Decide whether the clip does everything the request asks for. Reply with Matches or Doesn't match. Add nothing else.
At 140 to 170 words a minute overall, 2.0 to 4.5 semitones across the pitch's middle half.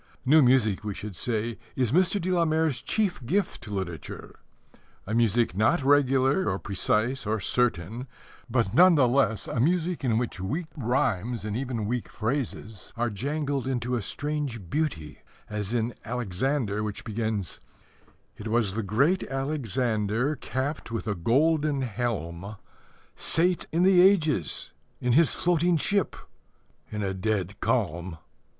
Doesn't match